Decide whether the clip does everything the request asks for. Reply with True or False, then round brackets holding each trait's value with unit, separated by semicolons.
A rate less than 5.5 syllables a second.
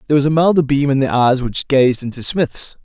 False (5.7 syllables/s)